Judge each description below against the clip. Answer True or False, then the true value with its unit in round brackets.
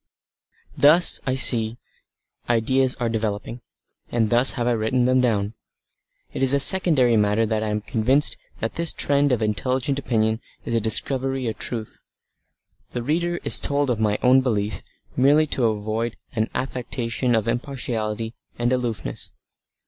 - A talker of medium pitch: False (120 Hz)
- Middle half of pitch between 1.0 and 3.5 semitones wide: True (3.1 semitones)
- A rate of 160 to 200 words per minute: False (150 wpm)